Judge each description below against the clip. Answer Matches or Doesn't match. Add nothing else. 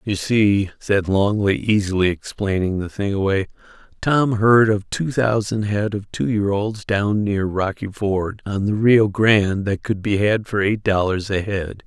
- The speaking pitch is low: Matches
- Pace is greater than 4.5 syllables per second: Doesn't match